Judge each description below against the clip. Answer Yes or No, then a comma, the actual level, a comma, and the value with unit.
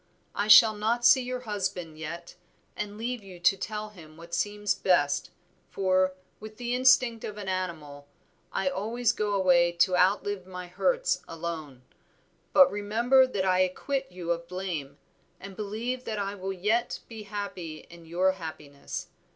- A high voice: Yes, high, 195 Hz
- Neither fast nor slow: Yes, average, 160 wpm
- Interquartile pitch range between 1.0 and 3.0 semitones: No, average, 3.8 semitones